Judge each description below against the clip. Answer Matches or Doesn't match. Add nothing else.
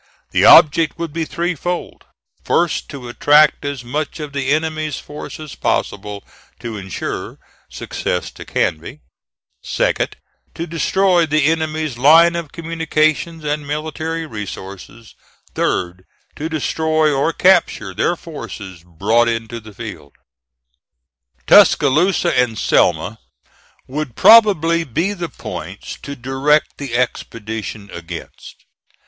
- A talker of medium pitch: Matches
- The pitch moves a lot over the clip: Matches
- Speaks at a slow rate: Matches